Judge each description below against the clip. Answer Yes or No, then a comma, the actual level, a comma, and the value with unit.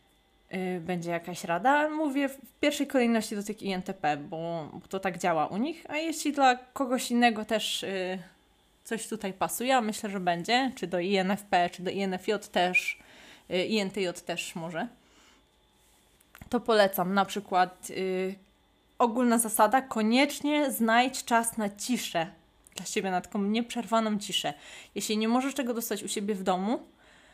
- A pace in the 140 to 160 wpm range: Yes, average, 145 wpm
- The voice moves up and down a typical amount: Yes, average, 4.8 semitones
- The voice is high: Yes, high, 205 Hz